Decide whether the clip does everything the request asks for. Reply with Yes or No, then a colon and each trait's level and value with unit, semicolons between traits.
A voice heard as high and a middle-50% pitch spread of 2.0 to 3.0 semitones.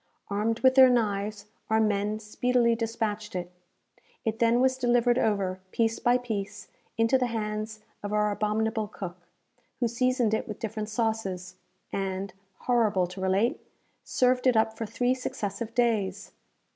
Yes: high, 220 Hz; narrow, 2.6 semitones